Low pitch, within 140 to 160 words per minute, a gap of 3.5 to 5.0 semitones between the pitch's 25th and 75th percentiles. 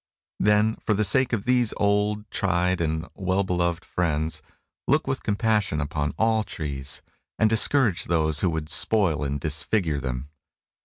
No: very low, 90 Hz; average, 150 wpm; wide, 5.5 semitones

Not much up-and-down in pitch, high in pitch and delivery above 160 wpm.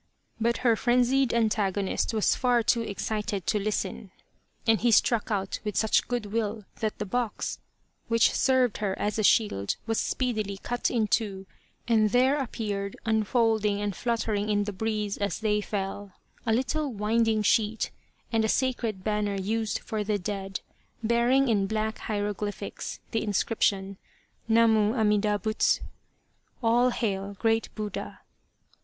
No: narrow, 2.1 semitones; high, 215 Hz; average, 150 wpm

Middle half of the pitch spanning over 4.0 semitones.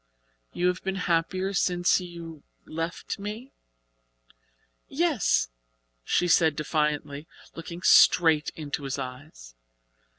No: average, 3.3 semitones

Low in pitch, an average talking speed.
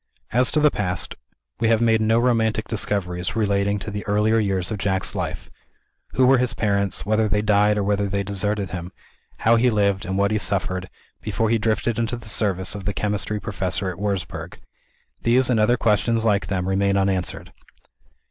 Yes: low, 105 Hz; average, 185 wpm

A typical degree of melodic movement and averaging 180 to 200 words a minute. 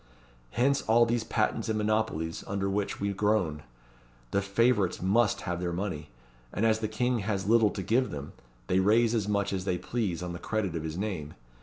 Yes: average, 3.4 semitones; average, 190 wpm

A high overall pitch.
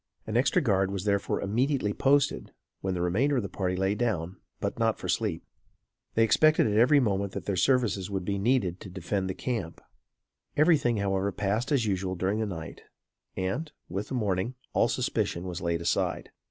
No: low, 100 Hz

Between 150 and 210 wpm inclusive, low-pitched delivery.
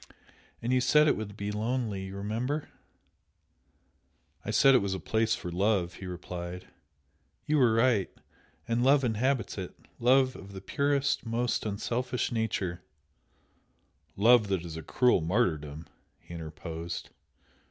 No: average, 140 wpm; low, 110 Hz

